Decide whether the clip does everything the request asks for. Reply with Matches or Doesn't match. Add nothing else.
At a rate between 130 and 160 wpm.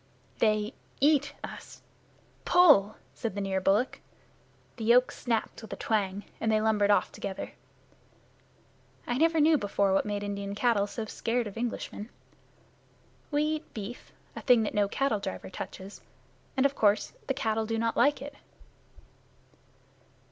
Matches